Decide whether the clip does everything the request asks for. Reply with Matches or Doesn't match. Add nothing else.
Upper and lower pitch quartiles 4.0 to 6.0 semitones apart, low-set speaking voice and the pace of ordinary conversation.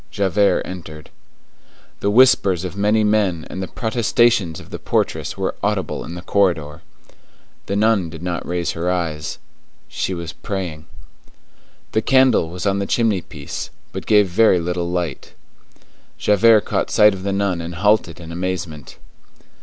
Doesn't match